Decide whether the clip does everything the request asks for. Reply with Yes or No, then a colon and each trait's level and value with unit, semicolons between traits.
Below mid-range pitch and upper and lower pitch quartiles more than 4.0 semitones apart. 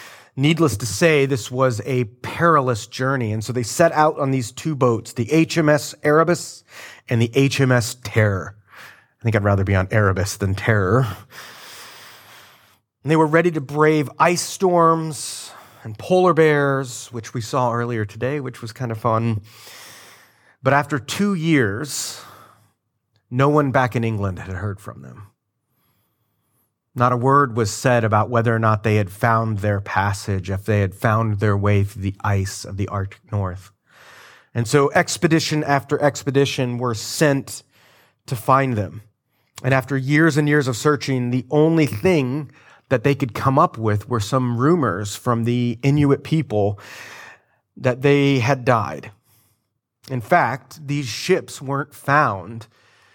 Yes: low, 125 Hz; average, 4.6 semitones